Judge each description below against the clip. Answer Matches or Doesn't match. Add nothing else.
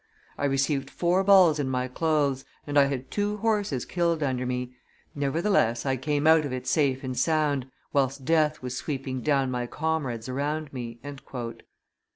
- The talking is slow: Doesn't match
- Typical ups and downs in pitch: Matches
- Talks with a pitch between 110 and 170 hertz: Matches